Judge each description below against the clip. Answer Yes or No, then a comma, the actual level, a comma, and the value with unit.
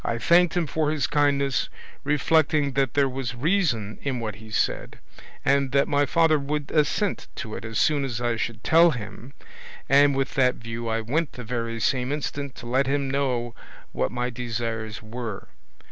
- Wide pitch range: No, average, 3.7 semitones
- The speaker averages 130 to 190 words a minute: Yes, average, 180 wpm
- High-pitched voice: No, low, 135 Hz